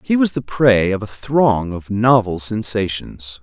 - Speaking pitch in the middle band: No, low, 110 Hz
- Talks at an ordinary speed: Yes, average, 175 wpm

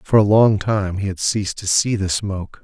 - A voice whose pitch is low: Yes, low, 100 Hz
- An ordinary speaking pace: No, fast, 250 wpm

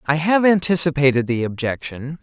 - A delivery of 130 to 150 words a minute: Yes, slow, 135 wpm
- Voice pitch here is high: No, medium, 150 Hz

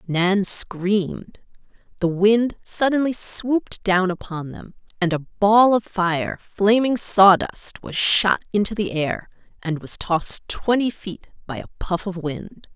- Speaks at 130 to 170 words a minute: Yes, average, 145 wpm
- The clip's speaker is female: Yes, female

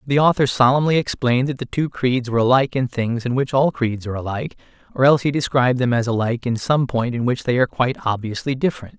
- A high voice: No, low, 125 Hz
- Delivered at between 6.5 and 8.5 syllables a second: Yes, 6.8 syllables/s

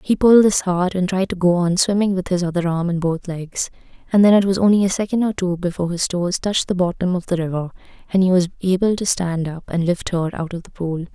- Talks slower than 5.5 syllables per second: No, 6.0 syllables/s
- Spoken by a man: No, female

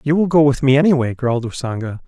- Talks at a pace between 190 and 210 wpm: No, fast, 230 wpm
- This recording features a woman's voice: No, male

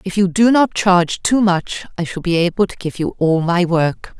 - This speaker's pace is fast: Yes, fast, 245 wpm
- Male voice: No, female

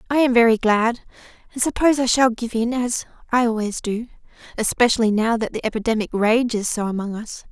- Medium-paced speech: Yes, average, 185 wpm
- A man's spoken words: No, female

